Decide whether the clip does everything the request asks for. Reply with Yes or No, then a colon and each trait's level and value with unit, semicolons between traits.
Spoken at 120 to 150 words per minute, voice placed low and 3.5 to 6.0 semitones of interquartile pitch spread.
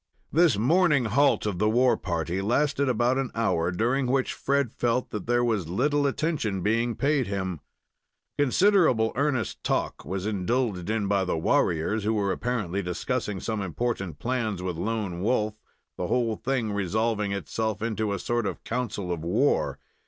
No: average, 160 wpm; low, 110 Hz; average, 4.4 semitones